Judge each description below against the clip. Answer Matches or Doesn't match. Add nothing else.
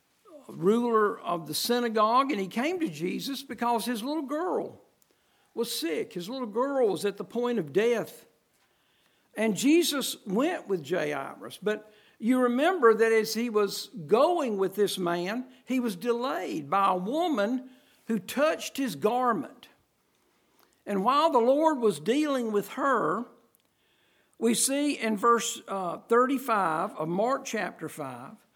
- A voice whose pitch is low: Doesn't match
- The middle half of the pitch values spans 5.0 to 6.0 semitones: Doesn't match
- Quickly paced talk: Doesn't match